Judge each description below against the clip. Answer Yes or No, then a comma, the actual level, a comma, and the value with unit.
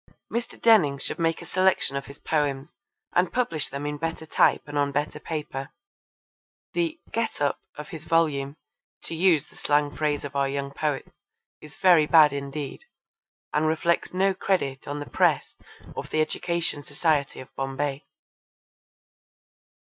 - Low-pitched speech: No, medium, 150 Hz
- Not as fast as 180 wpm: Yes, average, 155 wpm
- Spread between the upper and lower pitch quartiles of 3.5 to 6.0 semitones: No, average, 2.9 semitones